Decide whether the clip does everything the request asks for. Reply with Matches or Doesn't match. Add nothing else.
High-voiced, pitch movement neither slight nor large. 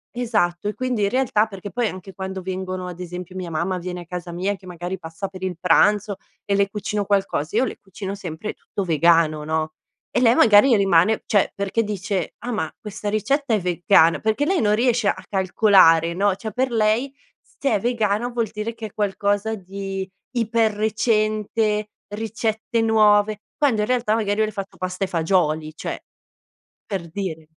Matches